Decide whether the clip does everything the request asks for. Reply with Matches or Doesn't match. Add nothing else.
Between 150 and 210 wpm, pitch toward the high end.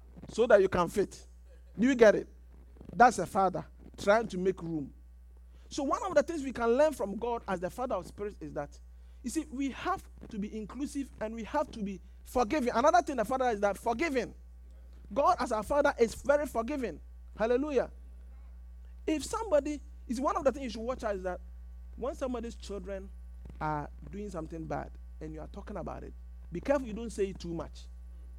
Matches